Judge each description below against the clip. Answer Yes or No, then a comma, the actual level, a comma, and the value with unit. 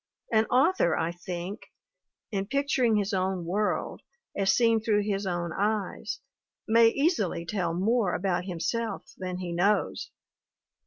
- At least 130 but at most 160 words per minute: Yes, average, 140 wpm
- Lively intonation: No, average, 3.9 semitones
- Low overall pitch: No, high, 200 Hz